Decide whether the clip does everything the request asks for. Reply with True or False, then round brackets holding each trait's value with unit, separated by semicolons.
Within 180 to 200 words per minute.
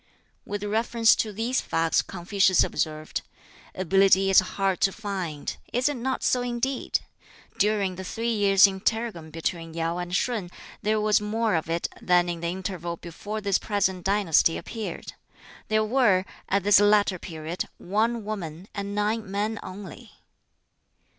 False (145 wpm)